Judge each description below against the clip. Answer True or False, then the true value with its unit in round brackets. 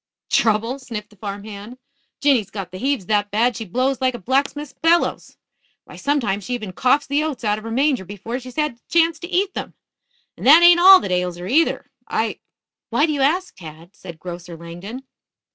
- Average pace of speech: False (210 wpm)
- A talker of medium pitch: False (240 Hz)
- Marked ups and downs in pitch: True (6.4 semitones)